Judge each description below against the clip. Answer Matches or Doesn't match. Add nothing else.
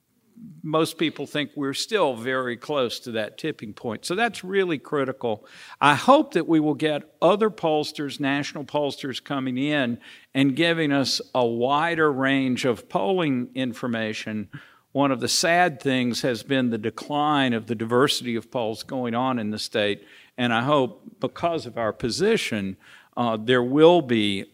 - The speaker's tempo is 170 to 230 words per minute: Doesn't match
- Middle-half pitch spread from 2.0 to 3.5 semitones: Doesn't match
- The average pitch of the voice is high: Doesn't match